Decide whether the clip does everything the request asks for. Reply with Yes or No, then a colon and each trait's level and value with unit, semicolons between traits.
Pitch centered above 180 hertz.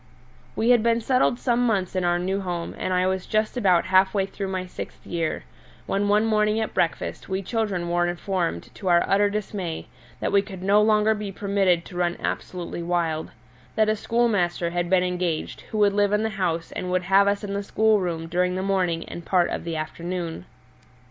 Yes: high, 190 Hz